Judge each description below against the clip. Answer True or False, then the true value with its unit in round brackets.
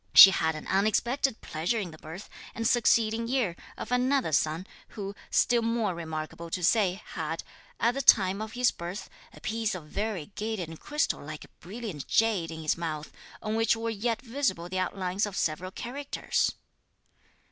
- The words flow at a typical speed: True (170 wpm)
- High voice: True (200 Hz)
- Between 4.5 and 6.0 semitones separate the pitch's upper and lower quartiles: True (5.3 semitones)